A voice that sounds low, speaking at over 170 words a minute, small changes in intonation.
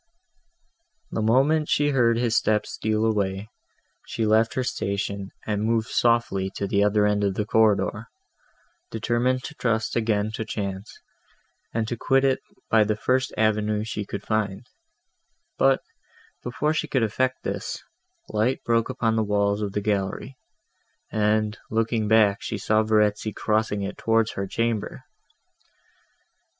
No: low, 110 Hz; average, 145 wpm; narrow, 2.0 semitones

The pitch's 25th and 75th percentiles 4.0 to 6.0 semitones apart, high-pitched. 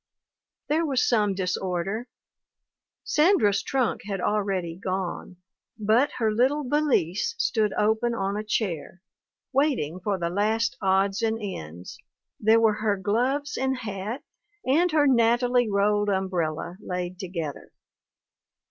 Yes: average, 4.5 semitones; high, 210 Hz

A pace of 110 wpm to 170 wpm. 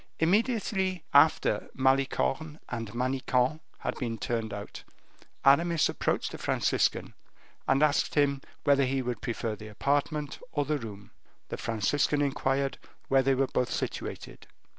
Yes: slow, 135 wpm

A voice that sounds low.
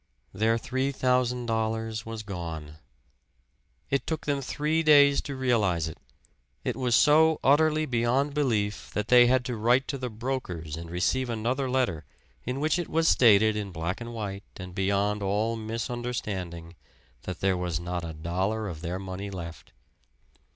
Yes: low, 110 Hz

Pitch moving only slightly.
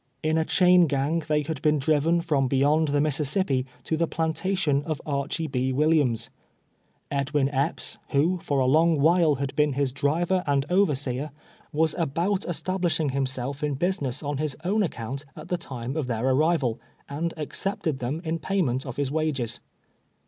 No: average, 3.2 semitones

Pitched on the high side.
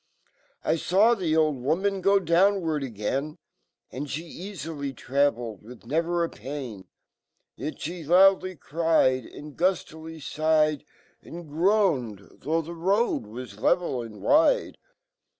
No: medium, 155 Hz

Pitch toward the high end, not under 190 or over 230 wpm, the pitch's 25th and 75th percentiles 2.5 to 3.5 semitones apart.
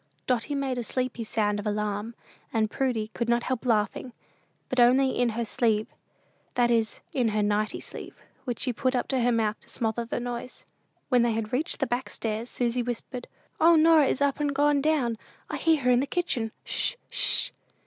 Yes: high, 245 Hz; average, 195 wpm; average, 2.8 semitones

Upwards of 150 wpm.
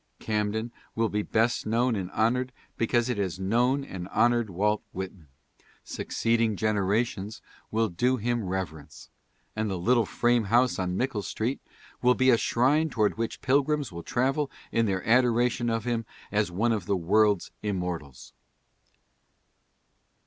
No: average, 145 wpm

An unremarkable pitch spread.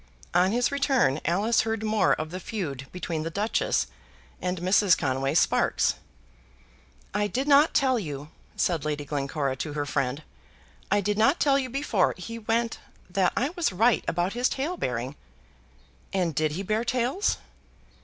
No: wide, 7.3 semitones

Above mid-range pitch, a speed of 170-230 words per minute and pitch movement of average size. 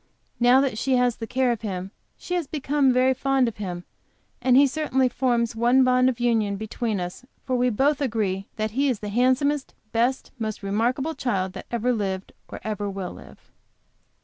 Yes: high, 240 Hz; average, 190 wpm; average, 3.9 semitones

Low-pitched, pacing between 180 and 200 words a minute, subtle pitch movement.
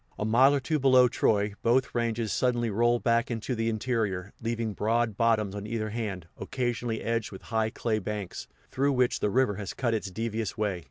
Yes: low, 115 Hz; average, 195 wpm; narrow, 2.2 semitones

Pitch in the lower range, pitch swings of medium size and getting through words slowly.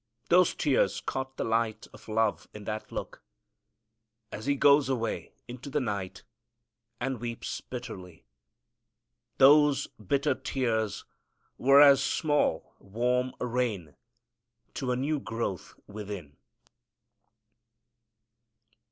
Yes: low, 125 Hz; average, 4.1 semitones; slow, 105 wpm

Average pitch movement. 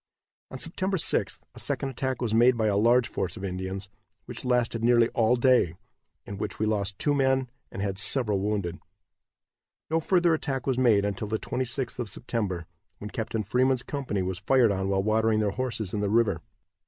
Yes: average, 4.2 semitones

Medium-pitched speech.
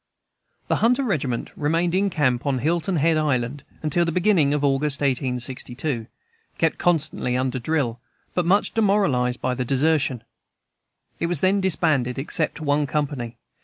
Yes: medium, 145 Hz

